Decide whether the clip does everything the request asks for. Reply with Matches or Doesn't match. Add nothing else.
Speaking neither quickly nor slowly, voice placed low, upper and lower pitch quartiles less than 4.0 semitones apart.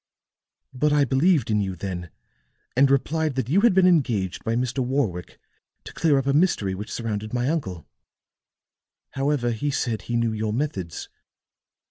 Doesn't match